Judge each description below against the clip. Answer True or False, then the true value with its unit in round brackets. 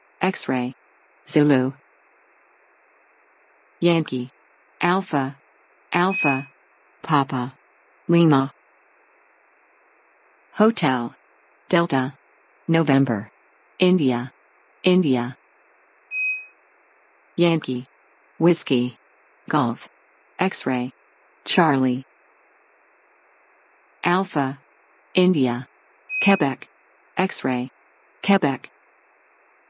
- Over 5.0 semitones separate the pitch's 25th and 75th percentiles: True (5.6 semitones)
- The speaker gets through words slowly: True (45 wpm)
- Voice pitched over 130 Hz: True (140 Hz)